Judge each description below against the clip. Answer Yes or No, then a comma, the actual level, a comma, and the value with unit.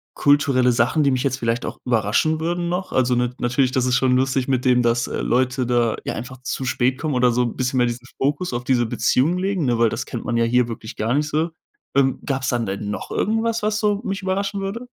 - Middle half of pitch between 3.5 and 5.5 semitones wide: Yes, average, 4.3 semitones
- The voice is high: No, low, 130 Hz